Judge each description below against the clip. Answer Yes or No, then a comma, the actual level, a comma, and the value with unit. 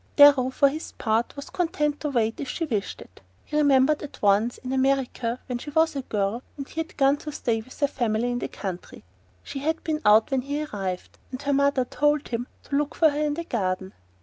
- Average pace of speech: No, fast, 230 wpm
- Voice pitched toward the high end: Yes, very high, 270 Hz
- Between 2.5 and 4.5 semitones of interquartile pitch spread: Yes, average, 4.2 semitones